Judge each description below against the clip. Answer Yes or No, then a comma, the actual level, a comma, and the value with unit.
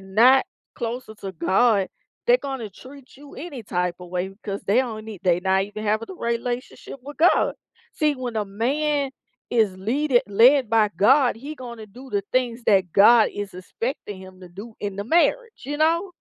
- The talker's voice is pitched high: Yes, high, 230 Hz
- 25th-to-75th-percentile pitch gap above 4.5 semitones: Yes, average, 5.2 semitones